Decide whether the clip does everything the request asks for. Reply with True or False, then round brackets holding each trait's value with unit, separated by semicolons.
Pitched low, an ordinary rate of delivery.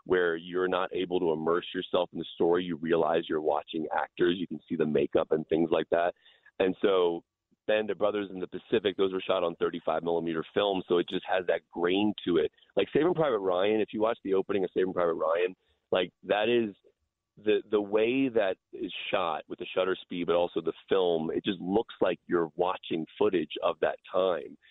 False (95 Hz; 215 wpm)